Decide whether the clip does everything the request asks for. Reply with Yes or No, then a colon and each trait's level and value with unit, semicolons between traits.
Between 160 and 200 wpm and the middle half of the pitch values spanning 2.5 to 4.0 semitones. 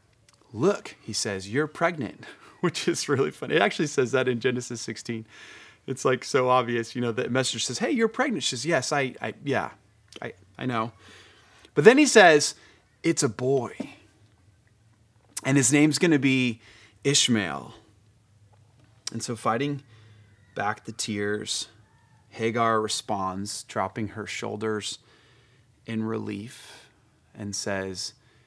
No: average, 140 wpm; average, 3.1 semitones